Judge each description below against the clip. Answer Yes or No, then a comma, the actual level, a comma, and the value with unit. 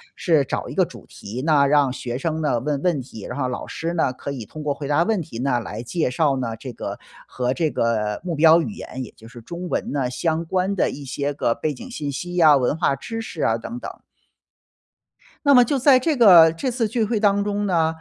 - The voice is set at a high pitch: No, medium, 150 Hz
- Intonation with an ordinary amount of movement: No, wide, 5.8 semitones